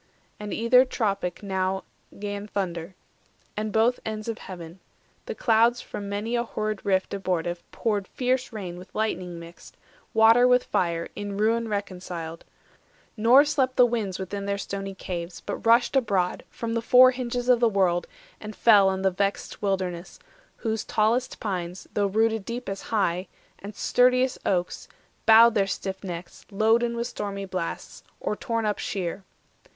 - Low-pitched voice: No, high, 205 Hz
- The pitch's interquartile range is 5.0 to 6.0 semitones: No, average, 3.5 semitones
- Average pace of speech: Yes, average, 160 wpm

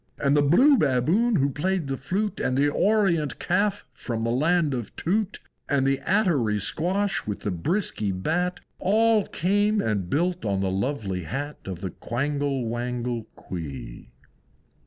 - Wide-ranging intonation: Yes, wide, 8.3 semitones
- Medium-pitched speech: Yes, medium, 145 Hz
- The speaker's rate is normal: Yes, average, 155 wpm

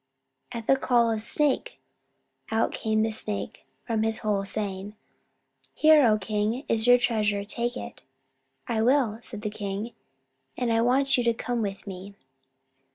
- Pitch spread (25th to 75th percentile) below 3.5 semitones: Yes, narrow, 2.5 semitones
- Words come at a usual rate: Yes, average, 160 wpm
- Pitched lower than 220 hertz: No, high, 225 Hz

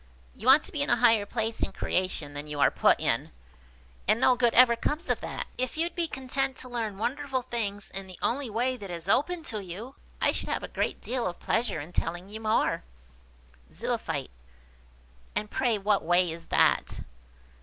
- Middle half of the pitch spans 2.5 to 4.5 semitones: No, average, 5.0 semitones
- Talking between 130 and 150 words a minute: No, average, 195 wpm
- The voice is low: No, high, 225 Hz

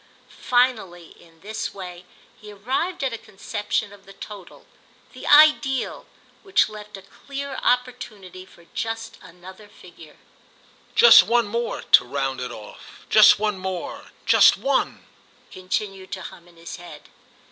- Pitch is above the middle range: Yes, high, 200 Hz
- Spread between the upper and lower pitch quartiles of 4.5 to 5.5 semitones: Yes, average, 4.8 semitones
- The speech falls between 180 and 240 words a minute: No, slow, 135 wpm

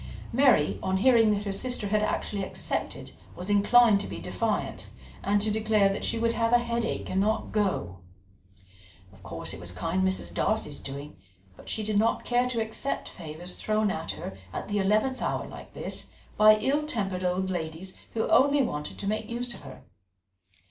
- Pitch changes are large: No, average, 3.6 semitones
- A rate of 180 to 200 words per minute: Yes, average, 185 wpm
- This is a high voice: Yes, high, 210 Hz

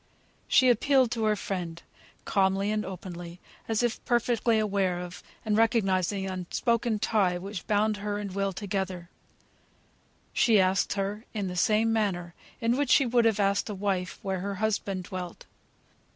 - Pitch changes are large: No, average, 2.8 semitones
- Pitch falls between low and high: No, high, 200 Hz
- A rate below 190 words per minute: Yes, average, 160 wpm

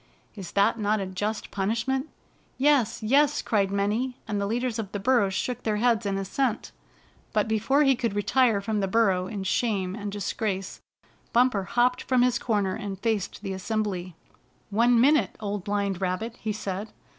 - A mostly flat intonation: No, average, 3.3 semitones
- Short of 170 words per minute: No, average, 175 wpm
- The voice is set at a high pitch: Yes, high, 215 Hz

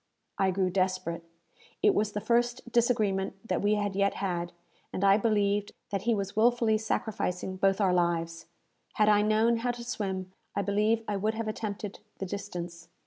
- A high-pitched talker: Yes, high, 205 Hz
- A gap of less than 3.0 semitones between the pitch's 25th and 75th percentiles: Yes, narrow, 2.6 semitones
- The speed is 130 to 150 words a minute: No, average, 175 wpm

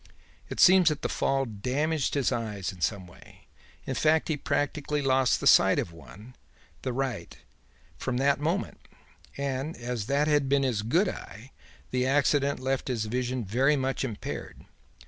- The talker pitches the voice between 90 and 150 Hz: Yes, low, 135 Hz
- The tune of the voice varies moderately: Yes, average, 3.4 semitones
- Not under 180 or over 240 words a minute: No, average, 165 wpm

